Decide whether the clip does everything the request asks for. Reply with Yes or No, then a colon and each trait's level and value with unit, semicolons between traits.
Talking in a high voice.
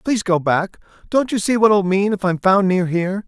Yes: high, 195 Hz